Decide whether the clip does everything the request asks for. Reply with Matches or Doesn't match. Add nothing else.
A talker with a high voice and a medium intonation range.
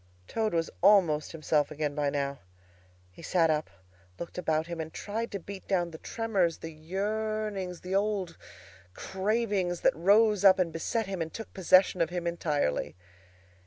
Doesn't match